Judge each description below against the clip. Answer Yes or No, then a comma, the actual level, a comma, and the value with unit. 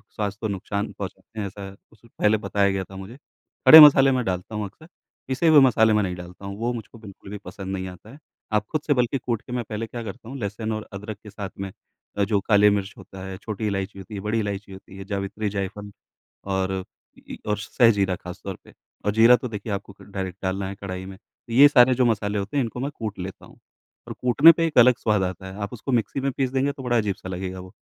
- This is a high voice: No, low, 105 Hz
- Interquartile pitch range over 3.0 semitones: Yes, average, 3.5 semitones